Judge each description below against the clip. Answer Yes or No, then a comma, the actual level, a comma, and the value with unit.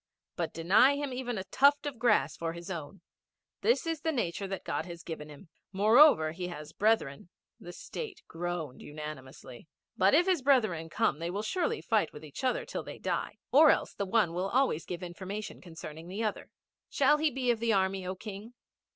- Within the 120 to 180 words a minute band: No, average, 200 wpm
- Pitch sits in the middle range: No, high, 195 Hz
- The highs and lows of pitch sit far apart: Yes, wide, 7.2 semitones